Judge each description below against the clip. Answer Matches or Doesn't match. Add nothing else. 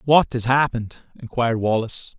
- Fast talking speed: Doesn't match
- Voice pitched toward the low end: Matches